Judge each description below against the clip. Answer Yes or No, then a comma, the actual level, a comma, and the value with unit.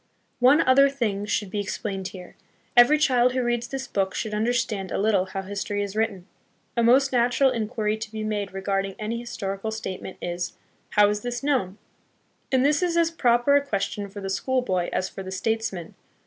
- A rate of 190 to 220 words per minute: Yes, average, 200 wpm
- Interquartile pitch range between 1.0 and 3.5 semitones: No, average, 4.0 semitones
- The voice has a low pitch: No, high, 220 Hz